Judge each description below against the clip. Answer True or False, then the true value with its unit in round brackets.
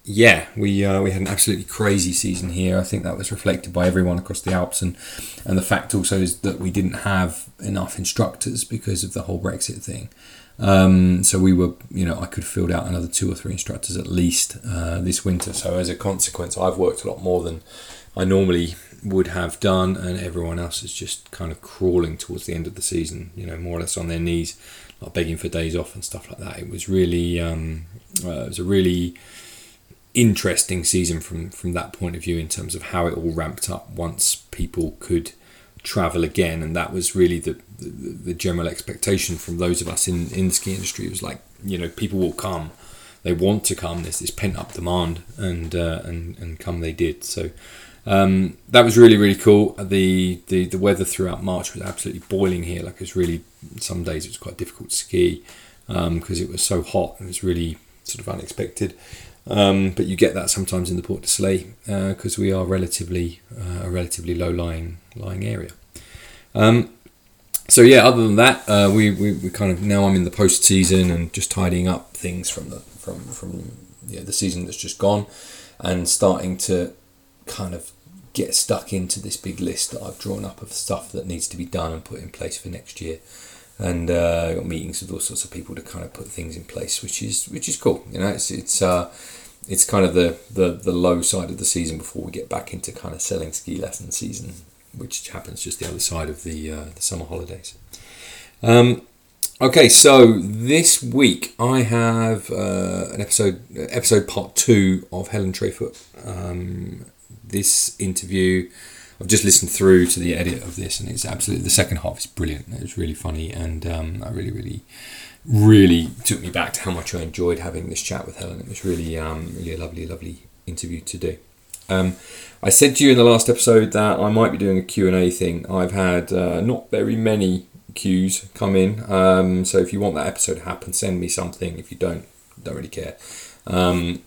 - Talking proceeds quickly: True (215 wpm)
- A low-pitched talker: True (95 Hz)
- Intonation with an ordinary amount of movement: False (2.3 semitones)